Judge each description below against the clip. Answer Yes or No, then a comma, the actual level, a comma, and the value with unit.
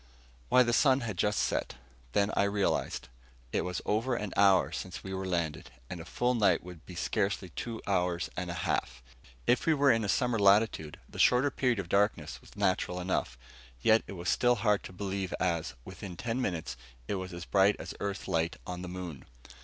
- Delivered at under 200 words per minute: No, fast, 205 wpm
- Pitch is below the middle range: Yes, very low, 95 Hz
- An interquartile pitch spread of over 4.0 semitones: No, average, 3.7 semitones